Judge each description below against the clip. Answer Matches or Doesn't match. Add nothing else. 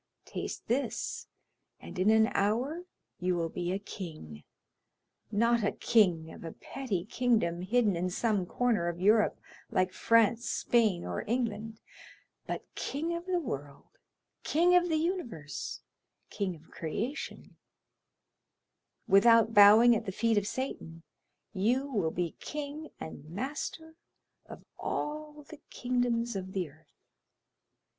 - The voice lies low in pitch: Doesn't match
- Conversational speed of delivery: Doesn't match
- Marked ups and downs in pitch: Matches